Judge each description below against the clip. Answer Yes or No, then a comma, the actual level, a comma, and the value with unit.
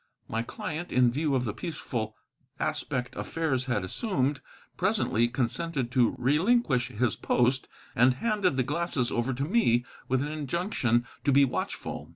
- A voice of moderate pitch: No, low, 130 Hz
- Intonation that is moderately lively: Yes, average, 4.8 semitones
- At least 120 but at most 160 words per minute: Yes, average, 150 wpm